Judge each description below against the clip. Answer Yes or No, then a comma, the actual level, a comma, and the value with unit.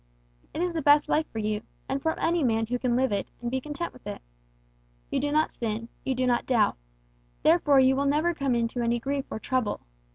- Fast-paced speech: Yes, fast, 225 wpm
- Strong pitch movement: No, average, 3.9 semitones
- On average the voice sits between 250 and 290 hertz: Yes, very high, 260 Hz